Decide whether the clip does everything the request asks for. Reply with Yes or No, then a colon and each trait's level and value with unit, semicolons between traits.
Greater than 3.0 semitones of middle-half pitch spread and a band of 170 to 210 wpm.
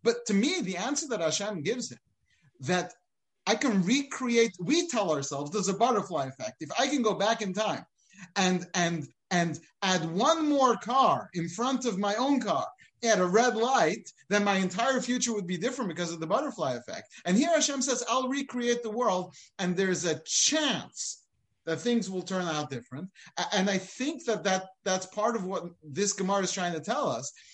Yes: average, 5.1 semitones; average, 195 wpm